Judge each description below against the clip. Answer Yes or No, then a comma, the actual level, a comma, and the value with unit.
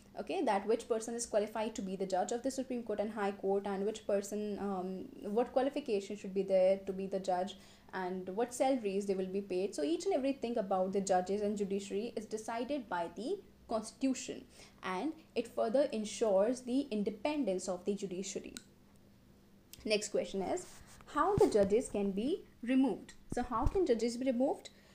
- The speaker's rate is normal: Yes, average, 180 wpm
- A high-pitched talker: Yes, high, 215 Hz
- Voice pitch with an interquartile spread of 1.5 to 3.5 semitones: No, average, 4.2 semitones